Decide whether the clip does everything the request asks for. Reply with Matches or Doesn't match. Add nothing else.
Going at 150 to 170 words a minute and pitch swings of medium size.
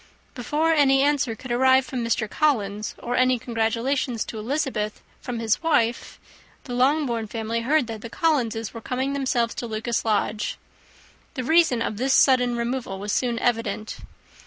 Matches